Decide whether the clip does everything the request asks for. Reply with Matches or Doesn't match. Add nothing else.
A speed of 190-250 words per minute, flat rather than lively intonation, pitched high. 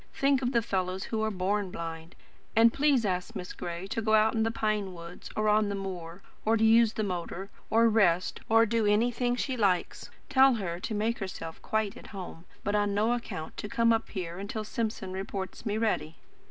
Doesn't match